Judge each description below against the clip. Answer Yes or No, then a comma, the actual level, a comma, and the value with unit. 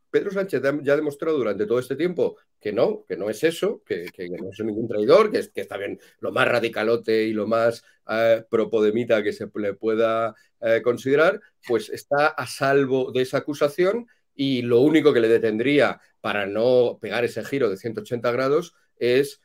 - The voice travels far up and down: Yes, wide, 8.5 semitones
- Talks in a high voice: No, low, 135 Hz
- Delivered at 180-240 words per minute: Yes, fast, 190 wpm